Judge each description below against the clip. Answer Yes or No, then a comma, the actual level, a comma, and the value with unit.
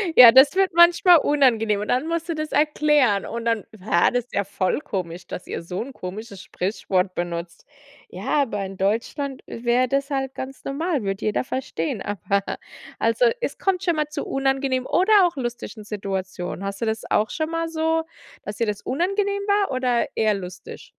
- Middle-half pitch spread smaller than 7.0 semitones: No, wide, 7.3 semitones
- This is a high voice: Yes, very high, 250 Hz